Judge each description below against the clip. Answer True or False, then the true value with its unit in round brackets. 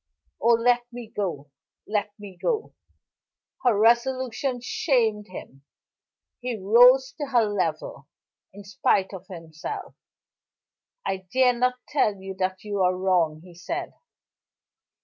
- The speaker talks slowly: True (125 wpm)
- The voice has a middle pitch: False (210 Hz)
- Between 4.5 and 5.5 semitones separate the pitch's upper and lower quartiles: True (4.8 semitones)